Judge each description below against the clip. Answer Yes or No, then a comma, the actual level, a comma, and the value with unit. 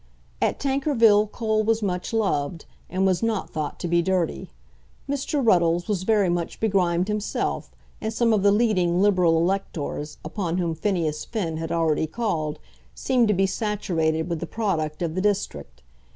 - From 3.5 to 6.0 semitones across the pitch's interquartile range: Yes, average, 4.6 semitones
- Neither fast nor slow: Yes, average, 165 wpm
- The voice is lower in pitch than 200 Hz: Yes, medium, 185 Hz